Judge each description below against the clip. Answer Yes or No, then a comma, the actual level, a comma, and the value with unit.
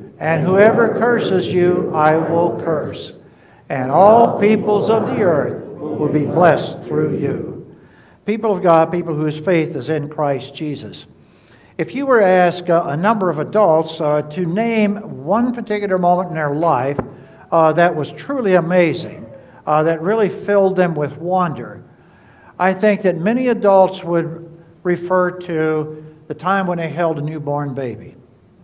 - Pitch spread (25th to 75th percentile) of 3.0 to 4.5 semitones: Yes, average, 3.9 semitones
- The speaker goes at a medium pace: Yes, average, 155 wpm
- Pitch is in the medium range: Yes, medium, 170 Hz